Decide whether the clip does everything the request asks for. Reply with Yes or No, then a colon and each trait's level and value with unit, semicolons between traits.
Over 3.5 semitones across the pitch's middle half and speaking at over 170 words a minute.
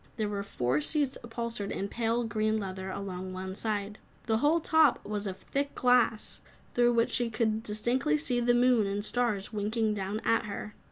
No: average, 3.2 semitones; average, 180 wpm